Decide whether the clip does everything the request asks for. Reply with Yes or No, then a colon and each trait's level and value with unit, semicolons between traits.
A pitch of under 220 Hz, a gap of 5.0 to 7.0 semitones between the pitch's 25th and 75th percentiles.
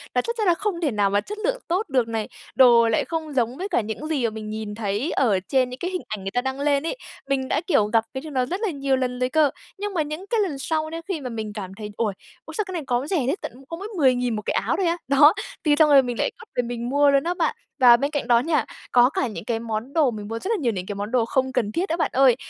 No: very high, 265 Hz; wide, 5.6 semitones